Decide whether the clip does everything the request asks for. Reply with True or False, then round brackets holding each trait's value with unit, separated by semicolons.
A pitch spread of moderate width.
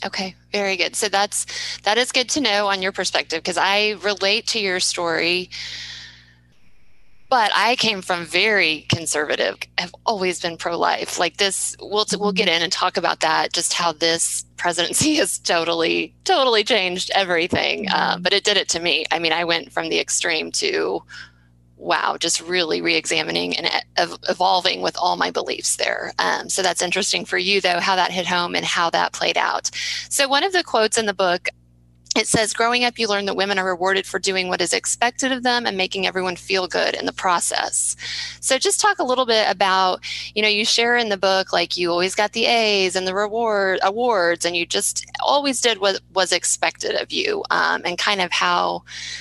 True (4.2 semitones)